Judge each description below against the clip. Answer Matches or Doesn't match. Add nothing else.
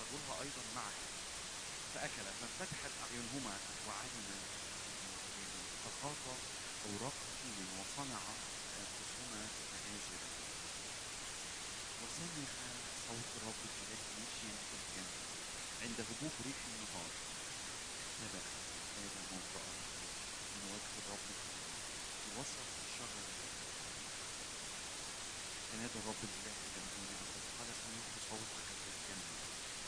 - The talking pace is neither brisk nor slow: Doesn't match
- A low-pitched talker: Matches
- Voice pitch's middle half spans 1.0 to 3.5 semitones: Matches